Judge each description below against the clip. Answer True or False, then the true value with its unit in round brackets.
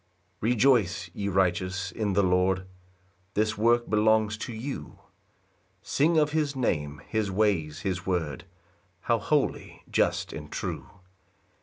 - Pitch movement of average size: True (4.2 semitones)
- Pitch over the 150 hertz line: False (100 Hz)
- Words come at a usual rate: False (130 wpm)